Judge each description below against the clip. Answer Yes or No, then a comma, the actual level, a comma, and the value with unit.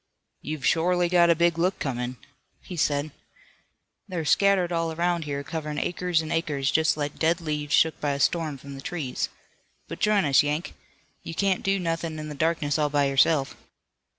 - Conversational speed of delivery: Yes, average, 180 wpm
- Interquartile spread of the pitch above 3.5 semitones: No, average, 2.9 semitones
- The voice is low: No, medium, 160 Hz